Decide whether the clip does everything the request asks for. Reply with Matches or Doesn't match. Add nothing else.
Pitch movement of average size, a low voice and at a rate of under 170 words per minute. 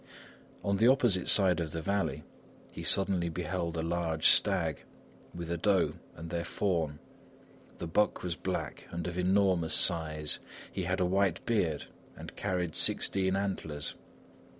Matches